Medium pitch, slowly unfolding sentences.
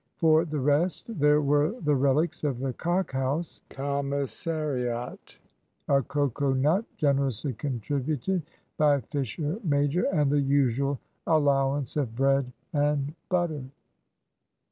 Yes: medium, 145 Hz; slow, 115 wpm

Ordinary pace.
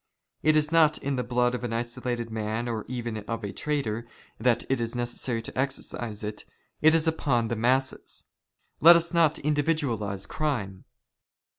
Yes: average, 180 wpm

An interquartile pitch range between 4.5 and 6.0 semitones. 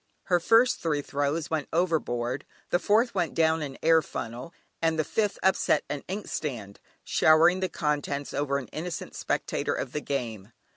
No: average, 3.8 semitones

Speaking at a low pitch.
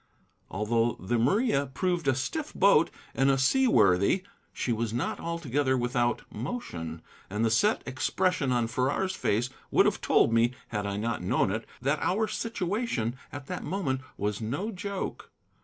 Yes: low, 130 Hz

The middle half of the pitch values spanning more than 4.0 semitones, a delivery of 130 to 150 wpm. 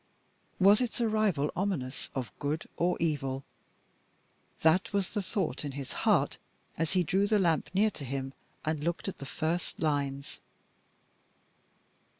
Yes: wide, 5.4 semitones; average, 145 wpm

